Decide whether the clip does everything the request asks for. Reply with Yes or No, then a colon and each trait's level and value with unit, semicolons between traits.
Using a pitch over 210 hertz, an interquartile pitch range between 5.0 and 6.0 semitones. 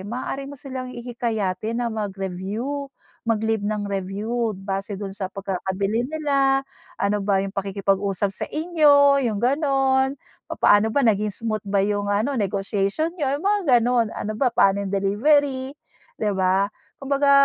Yes: high, 220 Hz; wide, 5.4 semitones